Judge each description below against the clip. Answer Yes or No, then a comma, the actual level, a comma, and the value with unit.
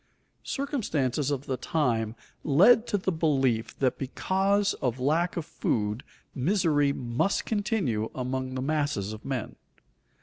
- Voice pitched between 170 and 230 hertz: No, medium, 140 Hz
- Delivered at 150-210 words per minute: No, slow, 135 wpm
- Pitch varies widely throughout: Yes, wide, 6.4 semitones